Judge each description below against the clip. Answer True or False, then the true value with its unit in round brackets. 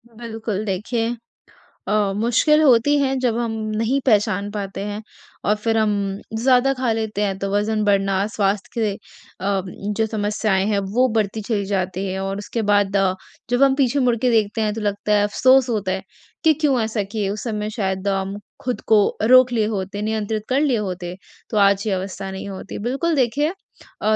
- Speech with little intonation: False (3.2 semitones)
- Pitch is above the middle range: True (215 Hz)